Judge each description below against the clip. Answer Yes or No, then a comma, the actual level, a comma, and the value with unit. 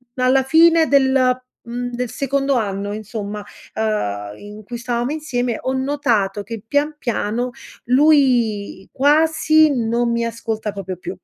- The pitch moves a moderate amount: Yes, average, 4.4 semitones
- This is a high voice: Yes, high, 245 Hz